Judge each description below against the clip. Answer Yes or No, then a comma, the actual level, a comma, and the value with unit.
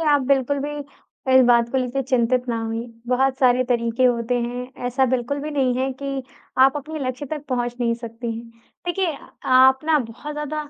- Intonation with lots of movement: No, narrow, 2.6 semitones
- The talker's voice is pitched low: No, very high, 255 Hz